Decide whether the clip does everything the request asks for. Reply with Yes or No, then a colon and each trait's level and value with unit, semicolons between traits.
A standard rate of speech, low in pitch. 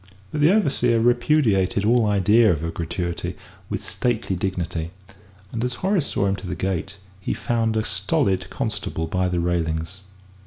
Yes: average, 160 wpm; low, 100 Hz